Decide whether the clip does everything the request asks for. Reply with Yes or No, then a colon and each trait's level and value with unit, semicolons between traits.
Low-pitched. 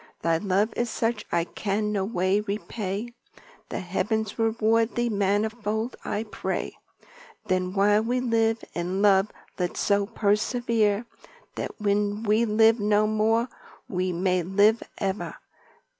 No: high, 210 Hz